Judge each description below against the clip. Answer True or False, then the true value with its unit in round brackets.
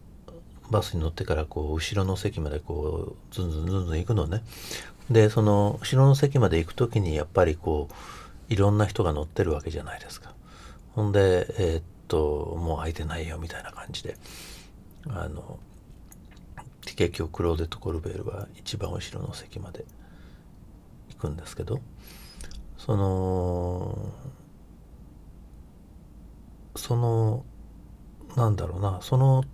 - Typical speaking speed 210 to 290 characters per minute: True (280 characters per minute)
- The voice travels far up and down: False (4.9 semitones)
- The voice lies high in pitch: False (95 Hz)